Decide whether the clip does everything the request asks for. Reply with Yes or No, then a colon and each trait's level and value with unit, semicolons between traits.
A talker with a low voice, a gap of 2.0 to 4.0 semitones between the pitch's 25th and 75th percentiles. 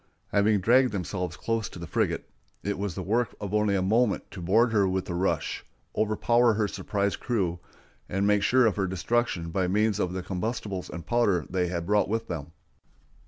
Yes: low, 100 Hz; average, 3.3 semitones